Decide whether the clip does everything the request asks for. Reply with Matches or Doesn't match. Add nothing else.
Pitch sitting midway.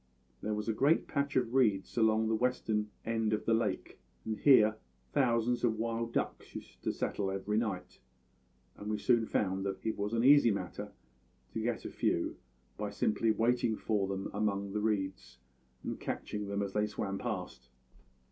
Doesn't match